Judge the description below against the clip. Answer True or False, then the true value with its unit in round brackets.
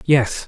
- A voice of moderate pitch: False (130 Hz)